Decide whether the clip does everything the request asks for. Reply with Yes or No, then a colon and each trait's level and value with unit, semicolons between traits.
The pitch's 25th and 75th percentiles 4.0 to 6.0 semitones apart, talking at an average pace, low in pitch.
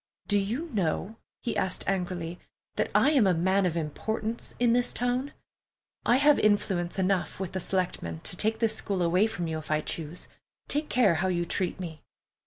No: average, 4.3 semitones; average, 190 wpm; high, 190 Hz